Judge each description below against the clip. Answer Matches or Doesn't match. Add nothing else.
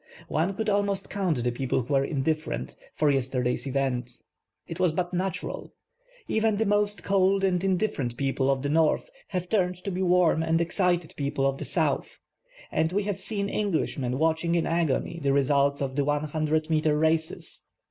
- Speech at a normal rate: Matches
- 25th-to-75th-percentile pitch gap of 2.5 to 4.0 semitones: Doesn't match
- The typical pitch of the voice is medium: Matches